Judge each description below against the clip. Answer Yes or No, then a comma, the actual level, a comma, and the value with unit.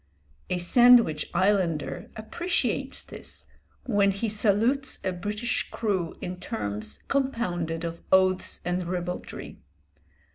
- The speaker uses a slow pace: Yes, slow, 105 wpm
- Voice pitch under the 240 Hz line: Yes, high, 190 Hz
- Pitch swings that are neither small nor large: Yes, average, 4.1 semitones